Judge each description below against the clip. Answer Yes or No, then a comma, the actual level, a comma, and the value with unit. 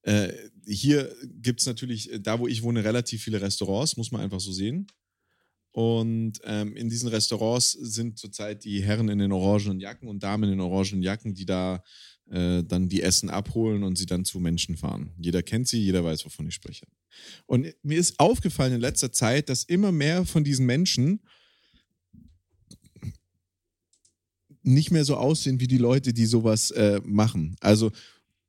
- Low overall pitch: Yes, low, 110 Hz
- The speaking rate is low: No, average, 170 wpm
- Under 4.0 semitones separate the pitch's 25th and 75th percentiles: No, average, 4.6 semitones